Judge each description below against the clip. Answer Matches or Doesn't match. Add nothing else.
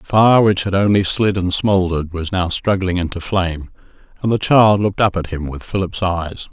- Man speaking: Matches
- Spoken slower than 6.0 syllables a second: Matches